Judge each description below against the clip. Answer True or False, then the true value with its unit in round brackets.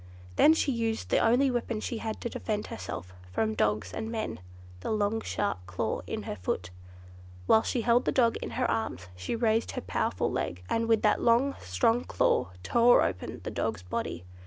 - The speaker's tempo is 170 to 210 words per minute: True (185 wpm)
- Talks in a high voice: True (220 Hz)